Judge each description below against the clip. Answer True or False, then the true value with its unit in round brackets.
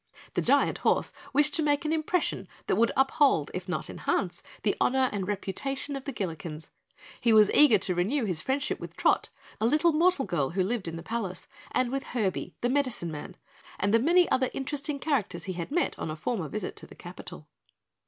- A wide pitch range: True (7.4 semitones)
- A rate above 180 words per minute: True (200 wpm)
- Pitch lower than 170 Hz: False (230 Hz)